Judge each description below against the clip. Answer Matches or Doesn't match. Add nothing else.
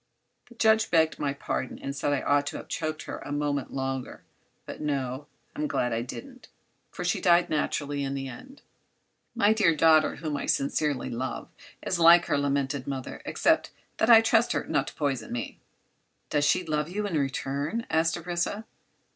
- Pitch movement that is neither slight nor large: Matches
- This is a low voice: Doesn't match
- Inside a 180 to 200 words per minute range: Matches